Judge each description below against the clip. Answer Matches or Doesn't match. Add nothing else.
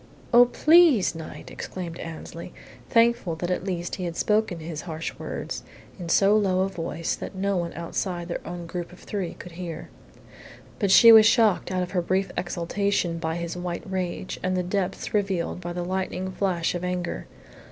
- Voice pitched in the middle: Matches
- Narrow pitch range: Matches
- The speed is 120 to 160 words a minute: Doesn't match